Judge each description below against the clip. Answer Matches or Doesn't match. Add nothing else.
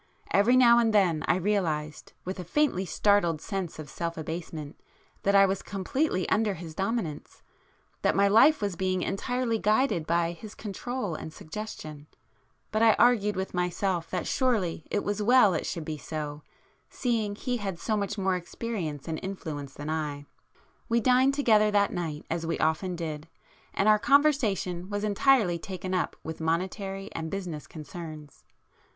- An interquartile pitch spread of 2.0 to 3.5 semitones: Doesn't match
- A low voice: Doesn't match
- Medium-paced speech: Matches